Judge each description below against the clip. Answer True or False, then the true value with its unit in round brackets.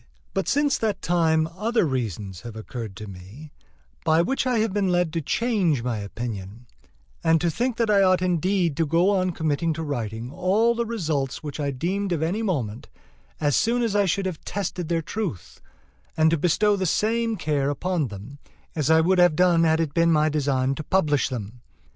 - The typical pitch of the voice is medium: True (165 Hz)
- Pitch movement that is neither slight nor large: False (5.7 semitones)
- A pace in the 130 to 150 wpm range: False (195 wpm)